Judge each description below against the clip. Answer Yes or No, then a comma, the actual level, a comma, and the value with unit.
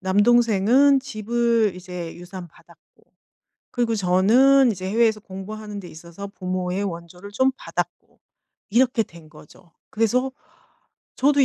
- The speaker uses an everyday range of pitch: Yes, average, 4.5 semitones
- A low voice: No, high, 205 Hz